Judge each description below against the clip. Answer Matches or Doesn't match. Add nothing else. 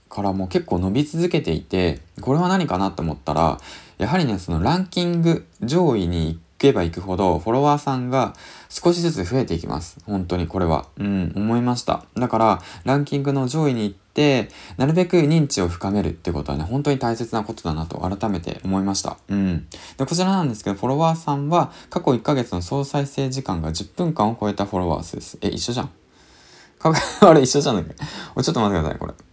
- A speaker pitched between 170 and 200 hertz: Doesn't match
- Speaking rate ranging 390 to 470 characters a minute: Matches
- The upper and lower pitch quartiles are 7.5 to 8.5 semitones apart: Matches